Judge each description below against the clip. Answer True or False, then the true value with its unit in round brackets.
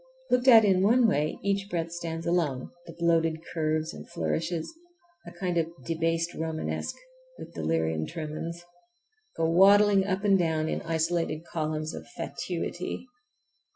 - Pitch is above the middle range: False (170 Hz)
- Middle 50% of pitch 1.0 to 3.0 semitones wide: False (3.4 semitones)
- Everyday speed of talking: False (130 wpm)